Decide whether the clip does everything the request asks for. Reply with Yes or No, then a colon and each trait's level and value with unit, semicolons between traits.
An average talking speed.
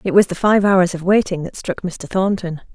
No: fast, 240 wpm